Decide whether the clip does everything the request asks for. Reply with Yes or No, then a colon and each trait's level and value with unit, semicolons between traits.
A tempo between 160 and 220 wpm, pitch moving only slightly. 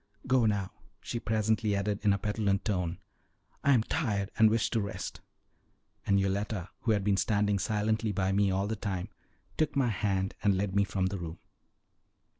Yes: average, 180 wpm; narrow, 2.2 semitones